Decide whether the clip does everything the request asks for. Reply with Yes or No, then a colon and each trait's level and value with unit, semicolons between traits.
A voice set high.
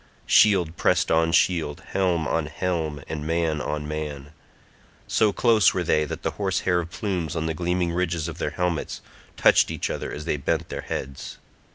No: very low, 80 Hz